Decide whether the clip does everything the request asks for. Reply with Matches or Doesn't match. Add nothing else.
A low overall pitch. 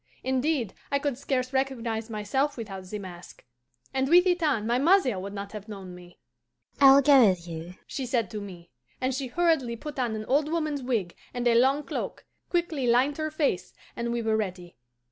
Doesn't match